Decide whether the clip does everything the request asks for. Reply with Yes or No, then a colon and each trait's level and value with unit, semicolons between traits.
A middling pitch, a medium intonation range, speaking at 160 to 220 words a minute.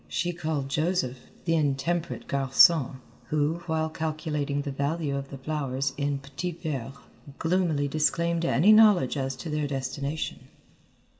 No: medium, 150 Hz; average, 3.2 semitones; slow, 135 wpm